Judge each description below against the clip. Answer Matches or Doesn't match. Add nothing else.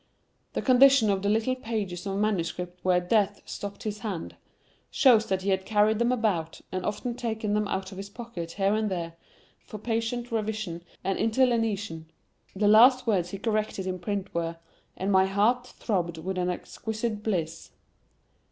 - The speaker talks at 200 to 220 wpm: Doesn't match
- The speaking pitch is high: Matches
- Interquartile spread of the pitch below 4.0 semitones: Matches